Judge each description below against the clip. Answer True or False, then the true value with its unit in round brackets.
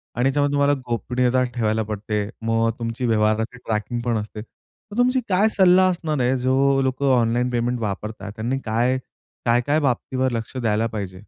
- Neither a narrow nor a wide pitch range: True (3.2 semitones)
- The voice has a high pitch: False (120 Hz)